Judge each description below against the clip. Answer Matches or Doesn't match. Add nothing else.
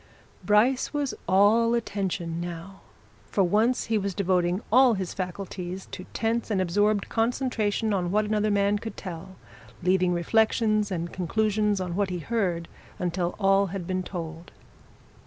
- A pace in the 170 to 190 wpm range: Doesn't match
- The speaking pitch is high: Matches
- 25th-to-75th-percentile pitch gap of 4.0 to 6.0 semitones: Doesn't match